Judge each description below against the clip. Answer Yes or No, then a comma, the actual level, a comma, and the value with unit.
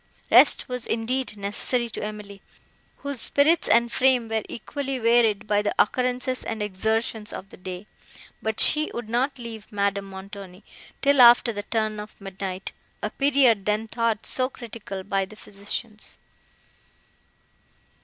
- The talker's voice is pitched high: Yes, high, 220 Hz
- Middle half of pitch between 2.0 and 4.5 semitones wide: Yes, average, 3.4 semitones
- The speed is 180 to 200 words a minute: No, average, 145 wpm